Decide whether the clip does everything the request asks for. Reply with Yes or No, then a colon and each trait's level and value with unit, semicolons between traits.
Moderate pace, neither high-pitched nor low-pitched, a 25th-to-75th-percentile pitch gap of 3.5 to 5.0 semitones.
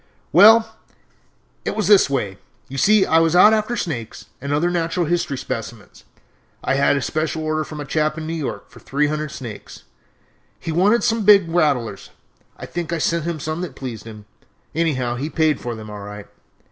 Yes: average, 190 wpm; medium, 155 Hz; average, 4.7 semitones